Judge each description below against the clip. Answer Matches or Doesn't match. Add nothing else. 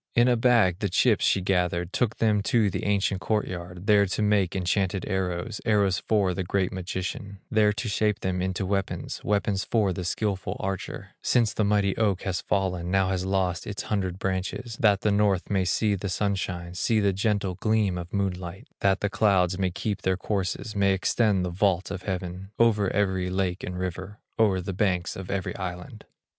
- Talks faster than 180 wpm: Matches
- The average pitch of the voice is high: Doesn't match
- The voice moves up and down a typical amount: Doesn't match